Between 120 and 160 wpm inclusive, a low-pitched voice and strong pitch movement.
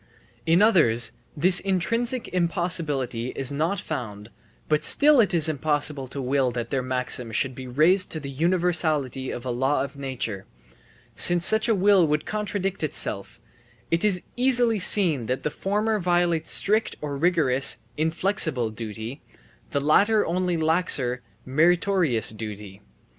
No: average, 140 wpm; medium, 155 Hz; wide, 6.1 semitones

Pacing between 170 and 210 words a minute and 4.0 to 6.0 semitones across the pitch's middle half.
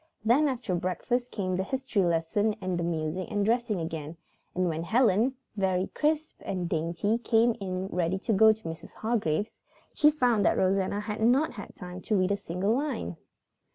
Yes: average, 180 wpm; average, 4.6 semitones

